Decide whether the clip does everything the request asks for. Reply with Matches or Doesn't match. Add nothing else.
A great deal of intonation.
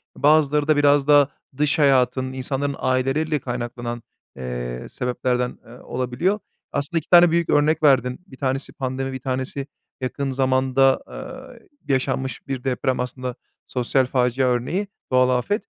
Doesn't match